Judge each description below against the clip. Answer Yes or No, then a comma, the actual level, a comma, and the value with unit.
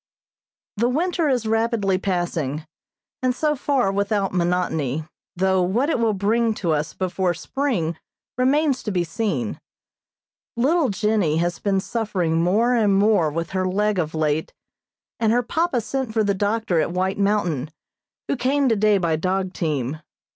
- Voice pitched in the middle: No, high, 200 Hz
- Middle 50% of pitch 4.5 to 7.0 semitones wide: Yes, average, 5.1 semitones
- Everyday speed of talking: Yes, average, 155 wpm